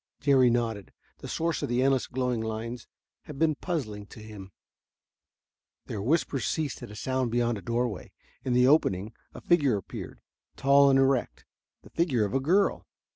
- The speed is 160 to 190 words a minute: Yes, average, 170 wpm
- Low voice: Yes, low, 125 Hz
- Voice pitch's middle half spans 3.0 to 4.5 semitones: Yes, average, 3.9 semitones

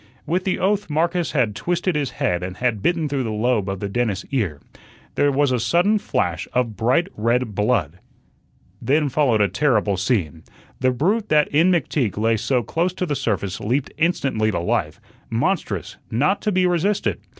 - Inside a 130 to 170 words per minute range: No, average, 180 wpm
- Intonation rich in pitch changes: Yes, wide, 7.9 semitones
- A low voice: Yes, low, 125 Hz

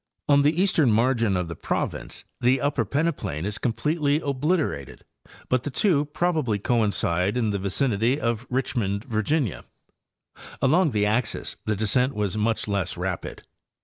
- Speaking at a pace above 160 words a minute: No, average, 150 wpm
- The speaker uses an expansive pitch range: Yes, wide, 5.7 semitones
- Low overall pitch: Yes, low, 120 Hz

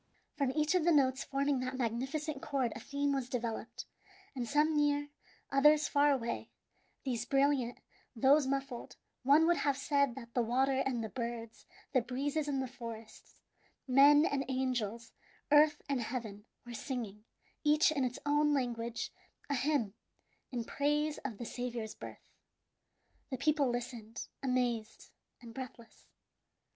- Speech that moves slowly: No, average, 145 wpm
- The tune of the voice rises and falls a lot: No, average, 3.3 semitones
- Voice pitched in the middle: No, very high, 265 Hz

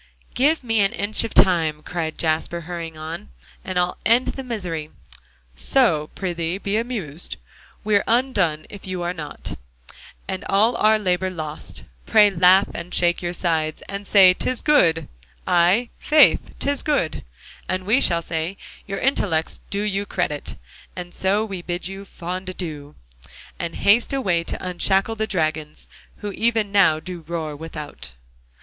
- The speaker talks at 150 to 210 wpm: Yes, average, 155 wpm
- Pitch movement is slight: No, average, 4.0 semitones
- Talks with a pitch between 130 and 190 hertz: Yes, medium, 185 Hz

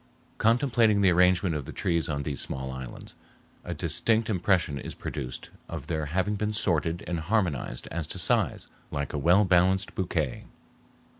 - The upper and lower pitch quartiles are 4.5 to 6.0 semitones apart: Yes, average, 5.1 semitones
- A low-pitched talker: Yes, very low, 85 Hz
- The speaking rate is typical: Yes, average, 160 wpm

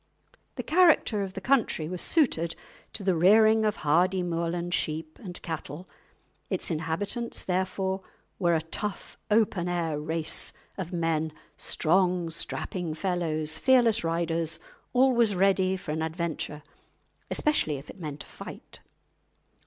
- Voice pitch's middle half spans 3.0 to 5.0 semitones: Yes, average, 3.5 semitones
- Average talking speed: No, slow, 130 wpm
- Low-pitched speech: No, medium, 175 Hz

